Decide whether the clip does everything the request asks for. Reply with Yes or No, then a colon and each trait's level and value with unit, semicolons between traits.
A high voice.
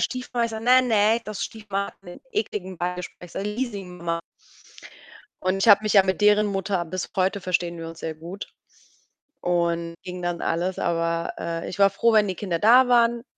Yes: high, 195 Hz